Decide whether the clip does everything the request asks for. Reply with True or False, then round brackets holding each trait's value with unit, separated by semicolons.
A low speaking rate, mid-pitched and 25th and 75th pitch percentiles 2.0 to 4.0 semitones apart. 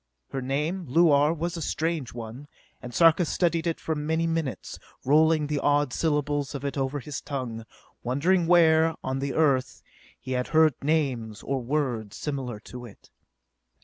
False (160 wpm; 145 Hz; 3.6 semitones)